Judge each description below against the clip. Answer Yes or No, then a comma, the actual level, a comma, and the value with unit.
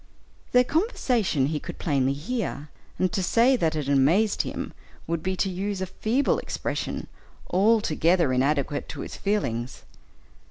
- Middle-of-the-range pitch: Yes, medium, 180 Hz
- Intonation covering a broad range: Yes, wide, 6.7 semitones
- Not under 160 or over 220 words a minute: No, average, 145 wpm